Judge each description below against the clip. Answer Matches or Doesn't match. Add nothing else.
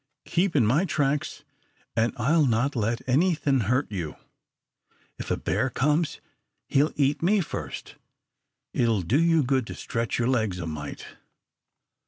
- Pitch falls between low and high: Doesn't match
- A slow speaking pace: Doesn't match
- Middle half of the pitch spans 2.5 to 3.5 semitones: Doesn't match